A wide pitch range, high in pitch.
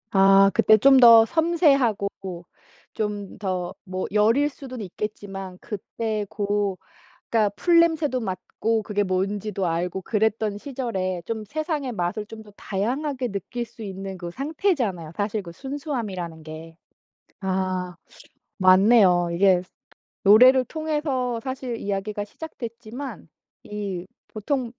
No: average, 4.8 semitones; high, 210 Hz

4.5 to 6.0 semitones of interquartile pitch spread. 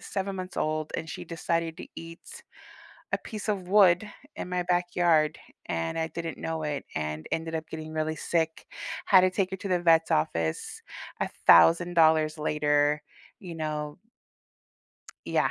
No: average, 2.7 semitones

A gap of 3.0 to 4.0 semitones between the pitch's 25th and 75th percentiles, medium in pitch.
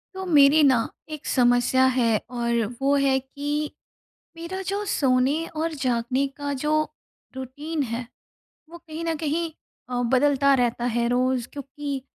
No: average, 3.5 semitones; very high, 275 Hz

